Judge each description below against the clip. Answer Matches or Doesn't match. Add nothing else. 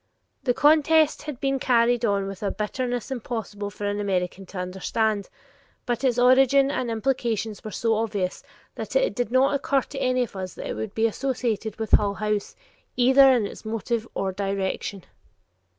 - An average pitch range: Matches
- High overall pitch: Matches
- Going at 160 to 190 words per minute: Matches